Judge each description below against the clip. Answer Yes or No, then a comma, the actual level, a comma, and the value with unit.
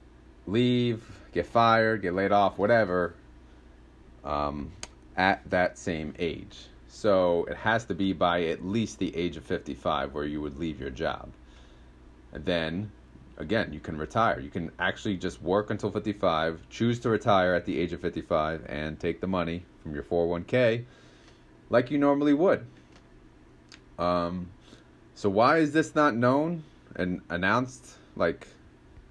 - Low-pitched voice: Yes, very low, 85 Hz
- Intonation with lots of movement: Yes, wide, 7.9 semitones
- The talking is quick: No, average, 150 wpm